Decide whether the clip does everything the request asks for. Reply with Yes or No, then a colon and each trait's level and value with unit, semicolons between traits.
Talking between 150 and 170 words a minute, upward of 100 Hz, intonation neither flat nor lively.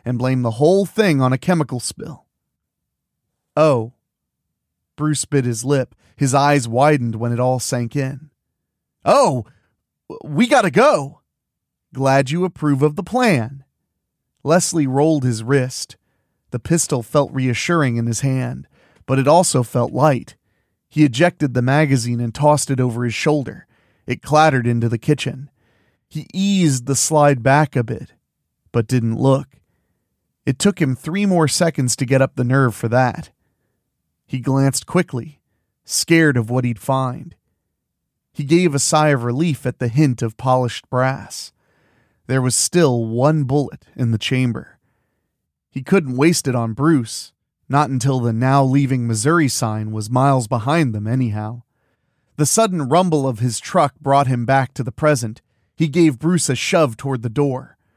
Yes: average, 160 wpm; low, 135 Hz; average, 3.9 semitones